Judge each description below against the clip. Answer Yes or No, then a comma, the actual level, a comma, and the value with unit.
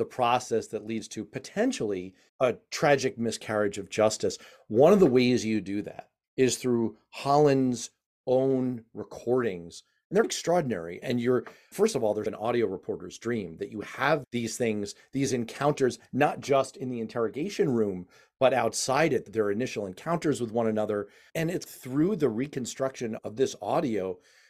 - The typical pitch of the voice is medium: No, low, 120 Hz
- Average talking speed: Yes, average, 160 wpm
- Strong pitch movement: No, average, 3.5 semitones